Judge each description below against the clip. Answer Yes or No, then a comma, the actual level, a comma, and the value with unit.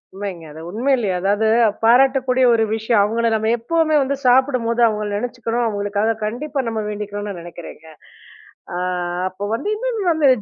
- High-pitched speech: Yes, high, 230 Hz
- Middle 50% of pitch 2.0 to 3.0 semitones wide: No, average, 4.1 semitones